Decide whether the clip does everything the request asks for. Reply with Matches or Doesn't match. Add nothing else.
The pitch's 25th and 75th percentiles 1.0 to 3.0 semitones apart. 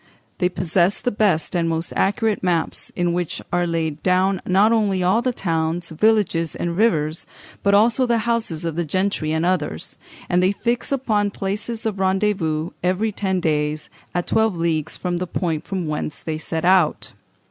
Doesn't match